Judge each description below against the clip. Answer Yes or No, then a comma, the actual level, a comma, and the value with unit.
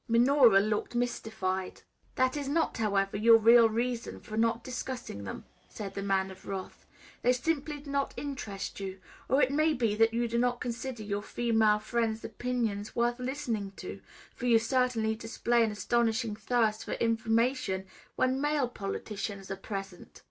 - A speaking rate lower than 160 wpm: No, average, 165 wpm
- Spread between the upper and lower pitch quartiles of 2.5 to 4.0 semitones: Yes, average, 3.2 semitones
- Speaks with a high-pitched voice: Yes, high, 230 Hz